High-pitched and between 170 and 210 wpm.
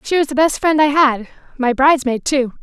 Yes: very high, 275 Hz; fast, 205 wpm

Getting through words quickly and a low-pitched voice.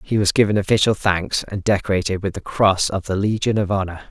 Yes: fast, 220 wpm; low, 100 Hz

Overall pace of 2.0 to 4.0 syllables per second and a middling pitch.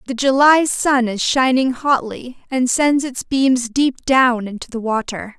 No: 3.9 syllables/s; very high, 255 Hz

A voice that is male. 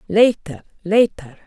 No: female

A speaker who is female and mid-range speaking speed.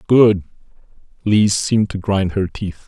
No: male; average, 145 wpm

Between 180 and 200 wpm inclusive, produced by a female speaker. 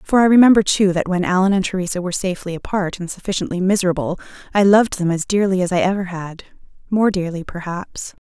Yes: average, 195 wpm; female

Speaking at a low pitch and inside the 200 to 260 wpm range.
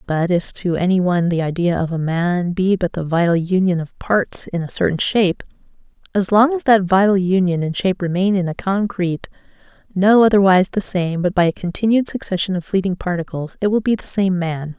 No: medium, 185 Hz; fast, 205 wpm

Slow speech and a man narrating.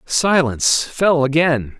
Yes: slow, 100 wpm; male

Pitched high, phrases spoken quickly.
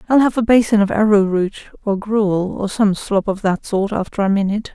Yes: high, 205 Hz; fast, 225 wpm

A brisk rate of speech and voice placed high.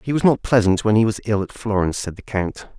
No: fast, 280 wpm; low, 105 Hz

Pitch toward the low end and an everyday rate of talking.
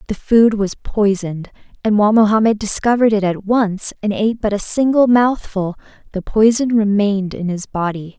No: high, 210 Hz; average, 170 wpm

